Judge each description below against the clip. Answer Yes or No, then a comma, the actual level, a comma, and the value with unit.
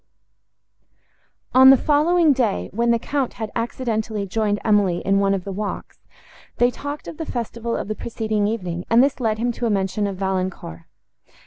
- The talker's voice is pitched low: No, high, 220 Hz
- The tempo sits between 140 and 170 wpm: No, average, 180 wpm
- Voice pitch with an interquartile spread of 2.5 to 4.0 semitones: Yes, average, 3.6 semitones